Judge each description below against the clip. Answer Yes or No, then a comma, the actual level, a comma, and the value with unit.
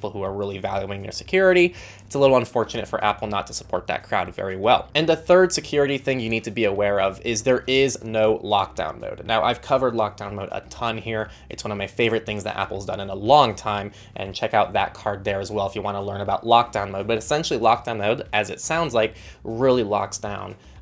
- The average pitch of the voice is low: Yes, low, 110 Hz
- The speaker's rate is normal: No, fast, 240 wpm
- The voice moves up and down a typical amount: Yes, average, 3.7 semitones